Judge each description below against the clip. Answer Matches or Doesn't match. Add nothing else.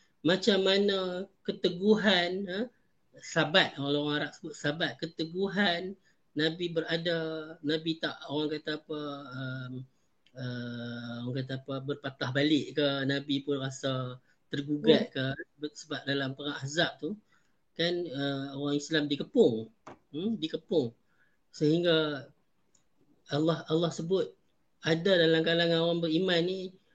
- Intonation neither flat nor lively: Matches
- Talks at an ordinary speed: Matches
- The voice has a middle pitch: Matches